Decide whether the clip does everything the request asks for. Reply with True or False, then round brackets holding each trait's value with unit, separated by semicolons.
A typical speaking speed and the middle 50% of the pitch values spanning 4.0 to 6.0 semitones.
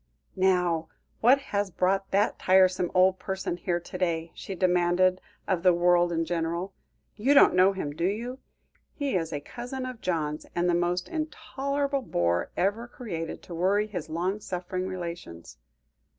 False (160 wpm; 3.0 semitones)